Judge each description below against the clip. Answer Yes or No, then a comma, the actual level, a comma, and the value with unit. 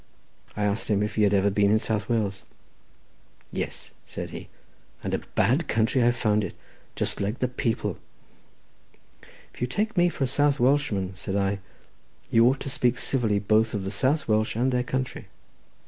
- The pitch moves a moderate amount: Yes, average, 4.0 semitones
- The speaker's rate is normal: Yes, average, 180 wpm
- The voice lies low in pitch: Yes, low, 115 Hz